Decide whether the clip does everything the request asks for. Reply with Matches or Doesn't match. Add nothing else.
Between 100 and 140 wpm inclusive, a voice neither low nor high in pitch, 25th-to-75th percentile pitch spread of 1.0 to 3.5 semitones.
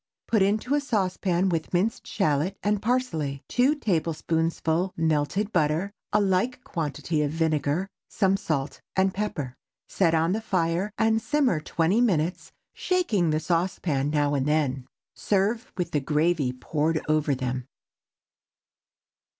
Doesn't match